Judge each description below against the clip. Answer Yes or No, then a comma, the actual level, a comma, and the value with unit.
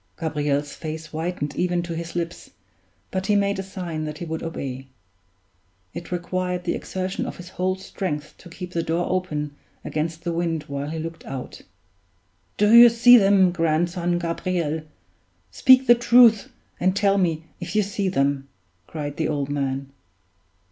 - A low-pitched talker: No, medium, 170 Hz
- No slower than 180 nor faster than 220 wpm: No, average, 160 wpm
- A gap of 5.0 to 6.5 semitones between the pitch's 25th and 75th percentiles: No, average, 3.3 semitones